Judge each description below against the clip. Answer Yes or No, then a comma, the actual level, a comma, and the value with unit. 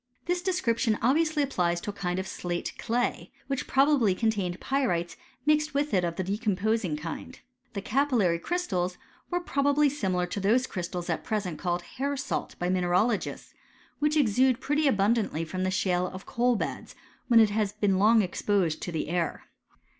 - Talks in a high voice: Yes, high, 210 Hz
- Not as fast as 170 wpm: No, average, 175 wpm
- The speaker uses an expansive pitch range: Yes, wide, 6.8 semitones